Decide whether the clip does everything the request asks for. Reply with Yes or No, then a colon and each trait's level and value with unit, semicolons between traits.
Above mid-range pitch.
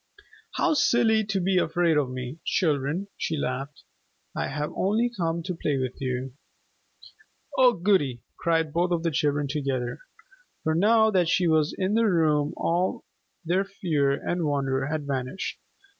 No: medium, 160 Hz